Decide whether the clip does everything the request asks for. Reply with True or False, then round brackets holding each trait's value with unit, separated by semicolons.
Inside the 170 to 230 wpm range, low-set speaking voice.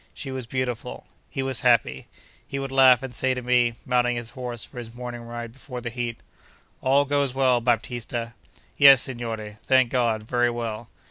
True (180 wpm; 120 Hz)